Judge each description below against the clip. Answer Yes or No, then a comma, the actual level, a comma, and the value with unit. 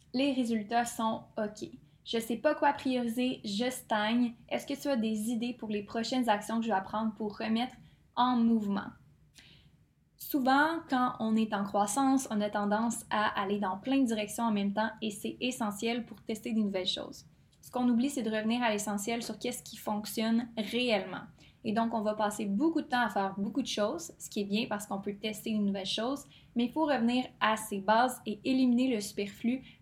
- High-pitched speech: Yes, high, 225 Hz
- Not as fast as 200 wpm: No, average, 210 wpm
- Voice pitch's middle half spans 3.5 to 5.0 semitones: No, average, 2.8 semitones